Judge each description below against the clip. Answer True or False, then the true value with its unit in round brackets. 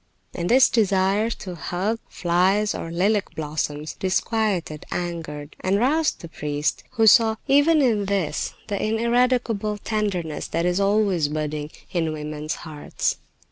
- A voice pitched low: False (190 Hz)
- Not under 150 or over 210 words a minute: False (135 wpm)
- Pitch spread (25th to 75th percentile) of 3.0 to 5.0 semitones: False (5.4 semitones)